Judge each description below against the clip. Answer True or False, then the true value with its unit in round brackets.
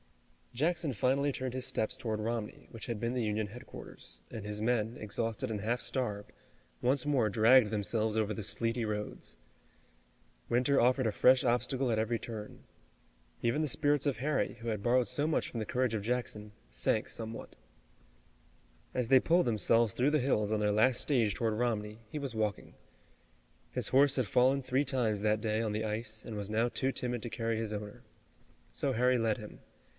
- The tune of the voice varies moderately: True (3.1 semitones)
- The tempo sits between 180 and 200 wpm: True (185 wpm)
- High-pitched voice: False (115 Hz)